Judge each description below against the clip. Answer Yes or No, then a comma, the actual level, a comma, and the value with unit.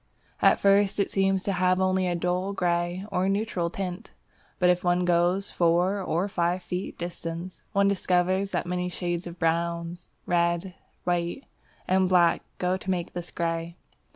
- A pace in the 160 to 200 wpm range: Yes, average, 165 wpm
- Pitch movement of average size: No, narrow, 1.5 semitones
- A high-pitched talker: No, medium, 180 Hz